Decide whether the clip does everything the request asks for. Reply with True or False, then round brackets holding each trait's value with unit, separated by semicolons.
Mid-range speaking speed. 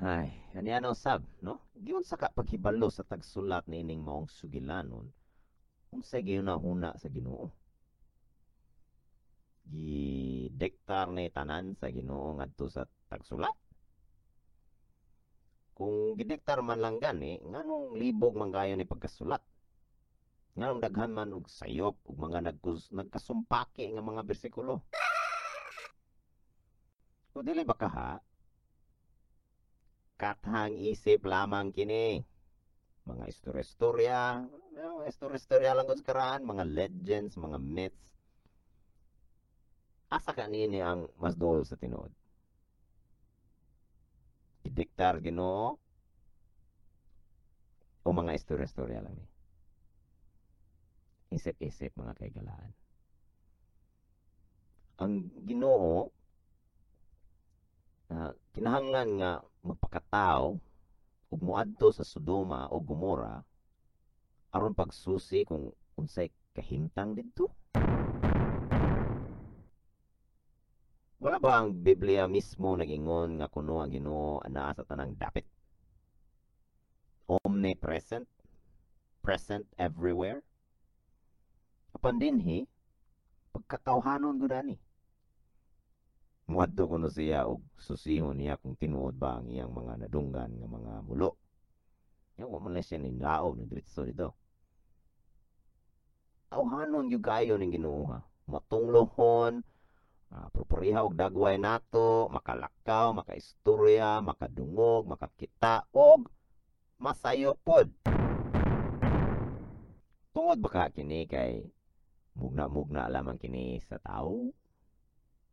False (95 wpm)